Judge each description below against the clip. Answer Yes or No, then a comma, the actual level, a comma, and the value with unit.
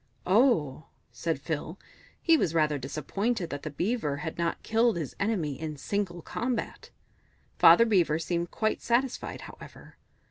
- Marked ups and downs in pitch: Yes, wide, 6.6 semitones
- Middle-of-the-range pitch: Yes, medium, 170 Hz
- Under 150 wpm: Yes, average, 140 wpm